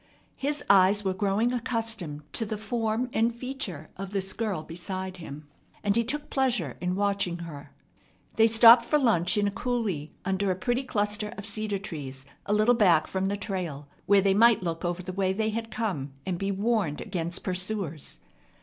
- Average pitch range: Yes, average, 3.9 semitones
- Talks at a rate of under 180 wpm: No, average, 185 wpm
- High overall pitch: Yes, high, 200 Hz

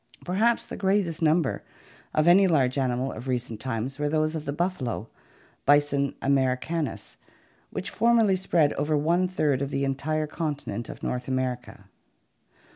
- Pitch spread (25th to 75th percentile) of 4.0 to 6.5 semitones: Yes, average, 4.6 semitones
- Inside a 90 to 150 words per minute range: Yes, average, 145 wpm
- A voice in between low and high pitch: Yes, medium, 145 Hz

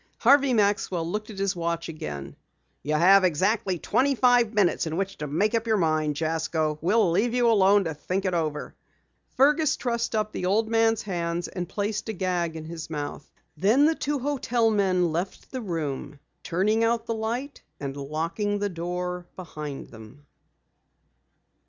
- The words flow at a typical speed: Yes, average, 170 wpm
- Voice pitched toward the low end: No, high, 190 Hz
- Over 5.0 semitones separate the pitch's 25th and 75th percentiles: Yes, wide, 5.5 semitones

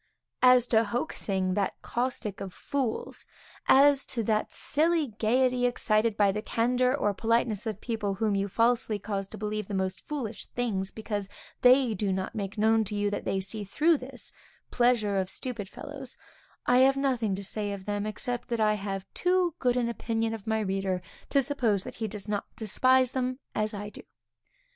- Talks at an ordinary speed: Yes, average, 185 wpm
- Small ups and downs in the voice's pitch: No, average, 3.6 semitones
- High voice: Yes, high, 220 Hz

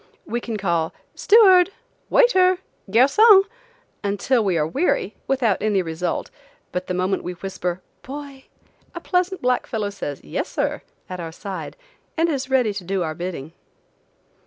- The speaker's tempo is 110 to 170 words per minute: Yes, average, 150 wpm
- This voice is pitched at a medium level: No, high, 205 Hz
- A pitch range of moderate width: No, wide, 7.6 semitones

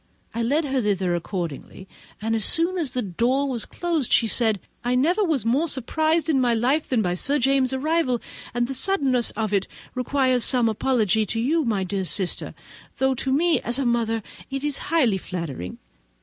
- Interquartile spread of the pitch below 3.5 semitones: No, average, 4.2 semitones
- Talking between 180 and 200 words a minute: Yes, average, 190 wpm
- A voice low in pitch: No, very high, 250 Hz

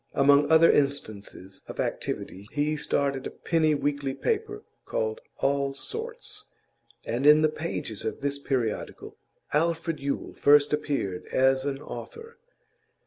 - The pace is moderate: No, slow, 130 wpm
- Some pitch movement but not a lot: Yes, average, 3.4 semitones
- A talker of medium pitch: Yes, medium, 145 Hz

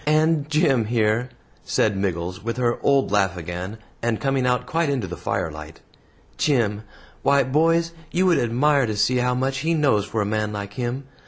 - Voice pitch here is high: No, low, 125 Hz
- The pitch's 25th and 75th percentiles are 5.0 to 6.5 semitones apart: Yes, wide, 5.4 semitones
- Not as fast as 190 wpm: Yes, average, 180 wpm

